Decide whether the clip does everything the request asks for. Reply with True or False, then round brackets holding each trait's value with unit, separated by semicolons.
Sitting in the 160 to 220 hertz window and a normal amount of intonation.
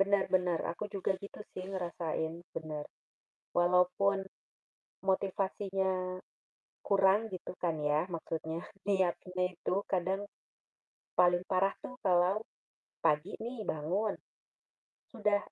False (185 Hz; 2.2 semitones)